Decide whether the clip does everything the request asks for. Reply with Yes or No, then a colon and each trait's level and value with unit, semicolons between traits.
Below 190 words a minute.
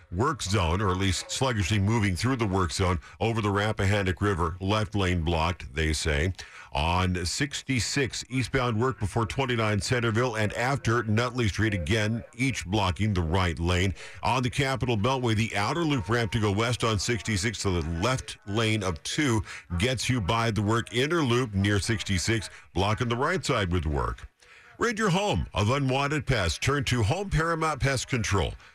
Yes: average, 175 wpm